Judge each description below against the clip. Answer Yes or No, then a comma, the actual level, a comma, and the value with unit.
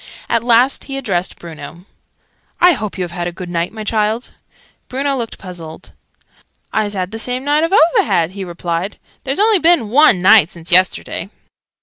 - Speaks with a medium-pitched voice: No, high, 210 Hz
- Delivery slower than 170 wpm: No, average, 175 wpm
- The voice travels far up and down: Yes, wide, 7.2 semitones